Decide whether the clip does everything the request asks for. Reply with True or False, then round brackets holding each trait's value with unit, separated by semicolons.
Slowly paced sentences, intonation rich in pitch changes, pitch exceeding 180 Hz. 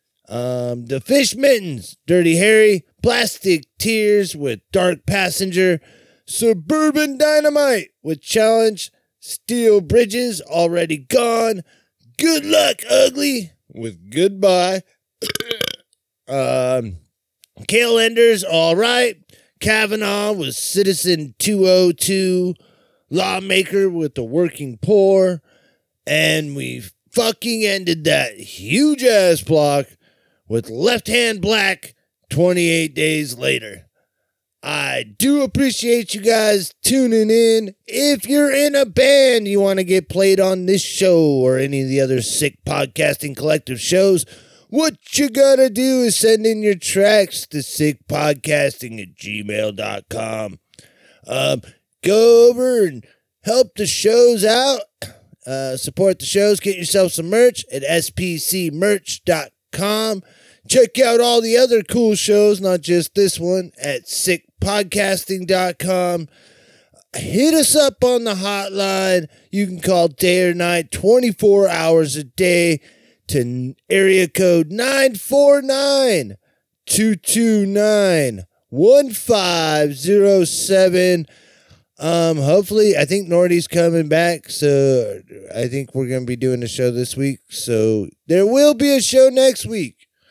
True (115 wpm; 6.5 semitones; 190 Hz)